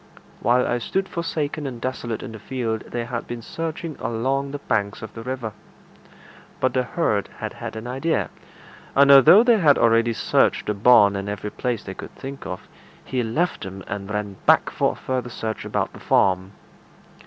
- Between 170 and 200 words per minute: Yes, average, 190 wpm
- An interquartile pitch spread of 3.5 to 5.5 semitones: Yes, average, 4.3 semitones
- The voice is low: Yes, low, 120 Hz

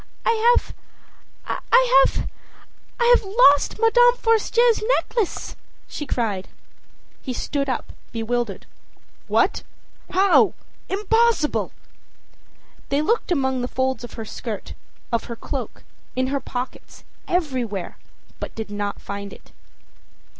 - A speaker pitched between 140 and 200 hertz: No, very high, 280 Hz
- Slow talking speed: Yes, slow, 110 wpm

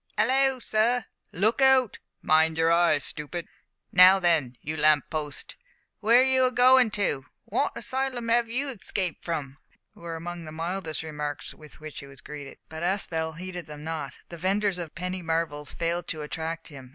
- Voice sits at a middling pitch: Yes, medium, 170 Hz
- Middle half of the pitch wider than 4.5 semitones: Yes, wide, 5.4 semitones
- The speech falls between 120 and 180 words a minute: Yes, average, 175 wpm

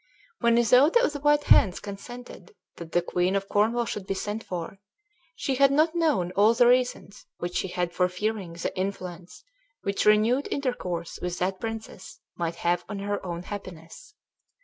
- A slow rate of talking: No, average, 170 wpm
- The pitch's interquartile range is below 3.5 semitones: No, average, 5.3 semitones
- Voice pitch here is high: Yes, high, 205 Hz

